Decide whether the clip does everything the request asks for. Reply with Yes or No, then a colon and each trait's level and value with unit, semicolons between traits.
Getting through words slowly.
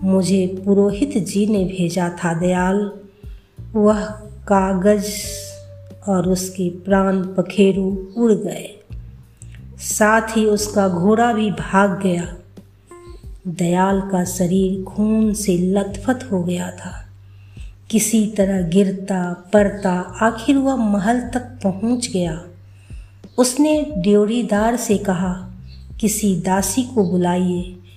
Yes: slow, 105 wpm